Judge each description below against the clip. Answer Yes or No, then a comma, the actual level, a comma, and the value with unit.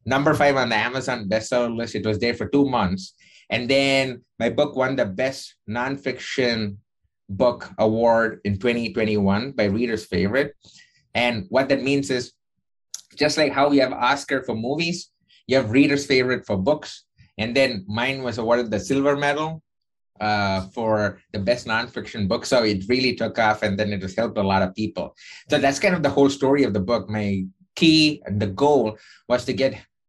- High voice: No, low, 125 Hz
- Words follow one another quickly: No, average, 190 wpm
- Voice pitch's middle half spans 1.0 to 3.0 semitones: No, average, 4.3 semitones